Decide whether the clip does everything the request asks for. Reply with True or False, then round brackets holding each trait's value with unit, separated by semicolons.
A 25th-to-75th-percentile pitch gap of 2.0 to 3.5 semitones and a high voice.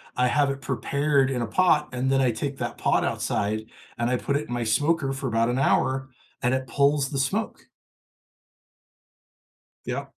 False (2.5 semitones; 135 Hz)